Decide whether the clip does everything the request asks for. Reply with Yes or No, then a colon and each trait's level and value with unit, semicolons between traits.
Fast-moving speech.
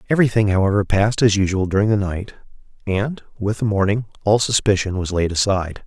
No: average, 175 wpm